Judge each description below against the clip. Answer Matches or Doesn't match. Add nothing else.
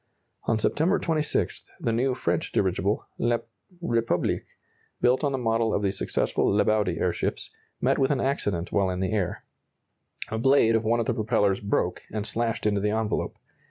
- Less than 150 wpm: Doesn't match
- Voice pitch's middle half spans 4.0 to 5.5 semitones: Doesn't match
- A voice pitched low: Matches